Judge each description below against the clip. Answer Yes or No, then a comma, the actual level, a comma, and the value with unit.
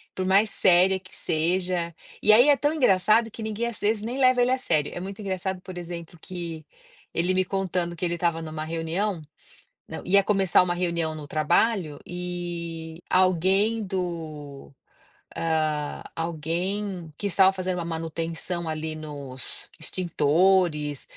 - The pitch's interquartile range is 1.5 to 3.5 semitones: Yes, average, 2.9 semitones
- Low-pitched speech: No, medium, 175 Hz